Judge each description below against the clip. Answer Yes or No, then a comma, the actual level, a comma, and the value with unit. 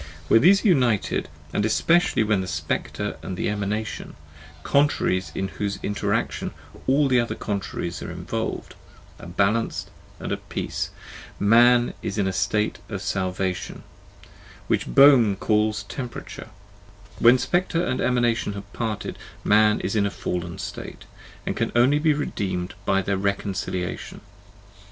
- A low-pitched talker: Yes, low, 105 Hz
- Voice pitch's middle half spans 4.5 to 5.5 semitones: No, average, 3.9 semitones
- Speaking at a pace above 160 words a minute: No, average, 140 wpm